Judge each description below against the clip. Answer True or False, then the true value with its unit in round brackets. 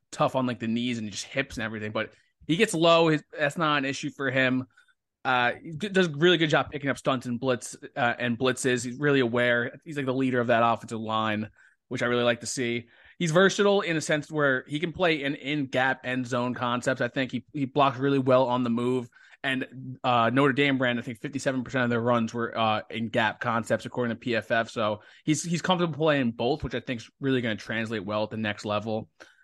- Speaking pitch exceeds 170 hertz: False (130 Hz)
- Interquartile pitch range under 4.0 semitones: True (3.5 semitones)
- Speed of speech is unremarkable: False (235 wpm)